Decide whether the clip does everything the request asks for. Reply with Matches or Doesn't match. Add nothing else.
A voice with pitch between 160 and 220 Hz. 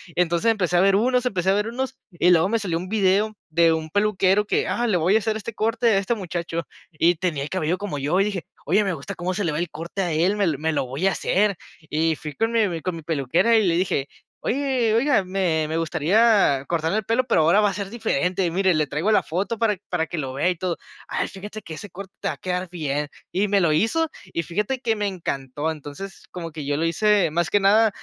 Matches